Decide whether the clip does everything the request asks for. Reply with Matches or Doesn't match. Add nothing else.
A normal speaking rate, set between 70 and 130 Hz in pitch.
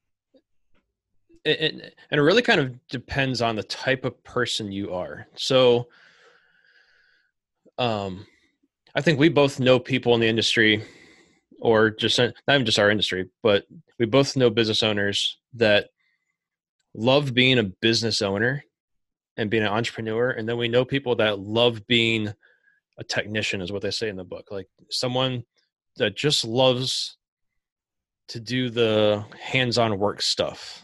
Matches